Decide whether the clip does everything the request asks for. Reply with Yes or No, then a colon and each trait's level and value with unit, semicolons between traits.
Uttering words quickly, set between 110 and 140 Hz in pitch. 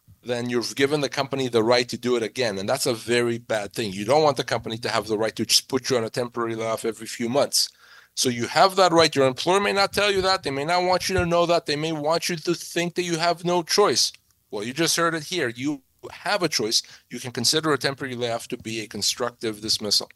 Yes: fast, 265 wpm; low, 130 Hz